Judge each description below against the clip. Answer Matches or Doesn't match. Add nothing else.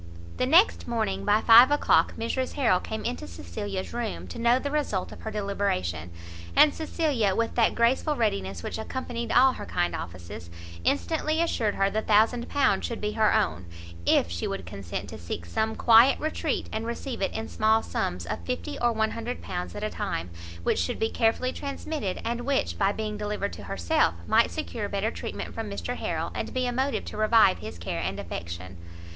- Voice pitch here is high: Matches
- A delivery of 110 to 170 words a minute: Doesn't match